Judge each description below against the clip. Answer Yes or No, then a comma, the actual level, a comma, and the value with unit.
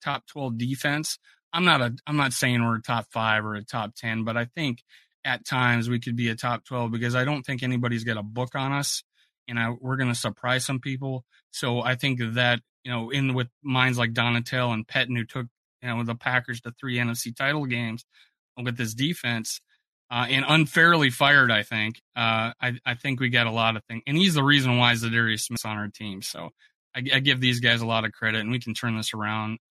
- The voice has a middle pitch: No, low, 120 Hz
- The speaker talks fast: Yes, fast, 230 wpm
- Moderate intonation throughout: No, narrow, 2.1 semitones